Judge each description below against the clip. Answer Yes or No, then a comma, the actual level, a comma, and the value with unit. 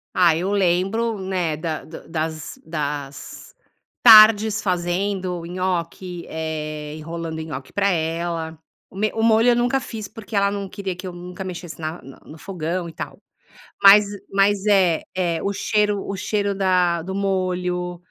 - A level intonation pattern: No, average, 3.3 semitones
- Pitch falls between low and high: Yes, medium, 180 Hz